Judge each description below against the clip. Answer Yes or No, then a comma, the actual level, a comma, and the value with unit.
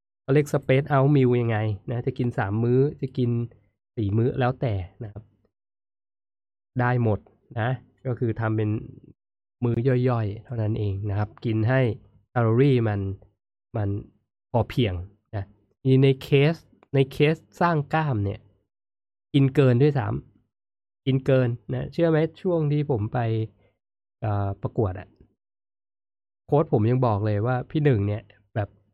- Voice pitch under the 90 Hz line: No, low, 115 Hz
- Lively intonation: No, average, 4.5 semitones